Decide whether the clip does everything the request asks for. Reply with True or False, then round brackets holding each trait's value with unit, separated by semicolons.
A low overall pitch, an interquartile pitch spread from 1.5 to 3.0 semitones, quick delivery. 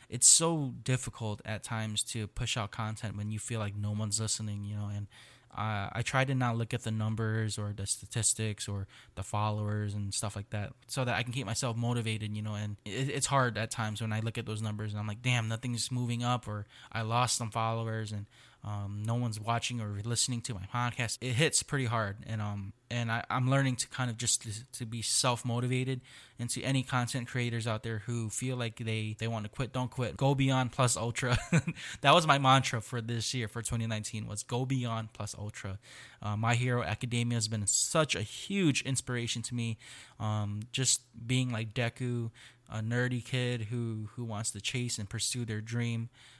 True (115 Hz; 2.4 semitones; 210 wpm)